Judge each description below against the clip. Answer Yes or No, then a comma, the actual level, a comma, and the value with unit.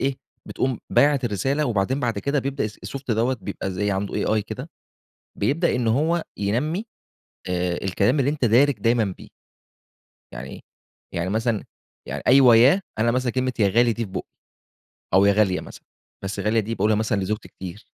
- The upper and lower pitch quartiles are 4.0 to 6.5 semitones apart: Yes, average, 4.6 semitones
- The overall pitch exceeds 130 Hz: No, low, 115 Hz